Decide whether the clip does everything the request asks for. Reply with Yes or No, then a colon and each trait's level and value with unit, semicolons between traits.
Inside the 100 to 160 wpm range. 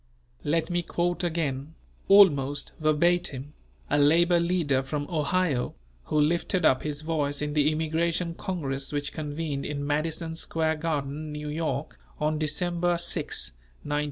Yes: slow, 135 wpm